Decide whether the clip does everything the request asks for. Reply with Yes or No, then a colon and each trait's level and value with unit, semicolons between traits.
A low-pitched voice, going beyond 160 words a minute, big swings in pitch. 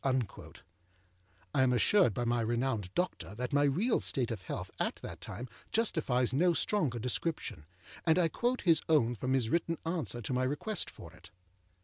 Yes: low, 130 Hz; average, 175 wpm; wide, 5.8 semitones